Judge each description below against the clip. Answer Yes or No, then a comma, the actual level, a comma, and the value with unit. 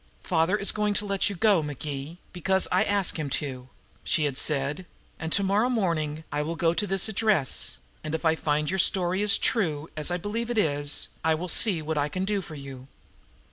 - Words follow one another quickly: Yes, fast, 215 wpm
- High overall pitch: No, medium, 170 Hz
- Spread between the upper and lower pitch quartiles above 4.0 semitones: Yes, average, 4.9 semitones